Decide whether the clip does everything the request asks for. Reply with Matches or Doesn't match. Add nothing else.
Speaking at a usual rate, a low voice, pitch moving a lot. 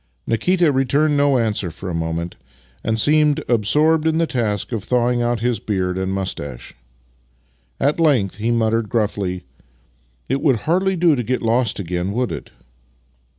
Matches